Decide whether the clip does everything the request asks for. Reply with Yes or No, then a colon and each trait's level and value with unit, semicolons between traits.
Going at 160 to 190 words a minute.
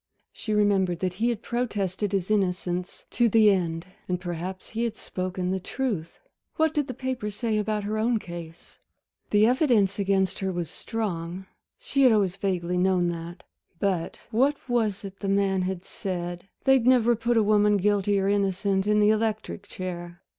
Yes: average, 175 wpm